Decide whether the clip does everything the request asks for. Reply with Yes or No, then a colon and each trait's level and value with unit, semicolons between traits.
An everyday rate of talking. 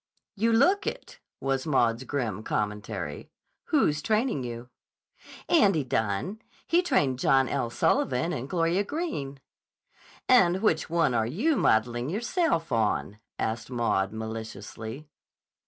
No: slow, 120 wpm